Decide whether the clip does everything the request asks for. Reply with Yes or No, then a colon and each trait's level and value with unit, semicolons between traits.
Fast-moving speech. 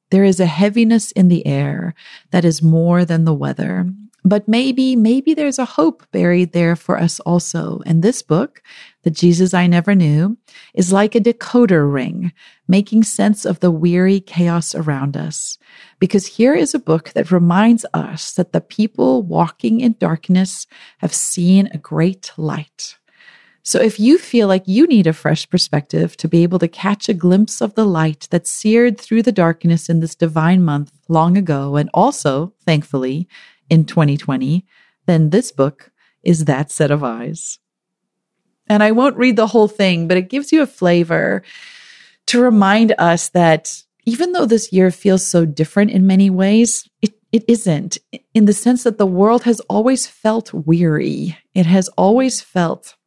No: average, 170 wpm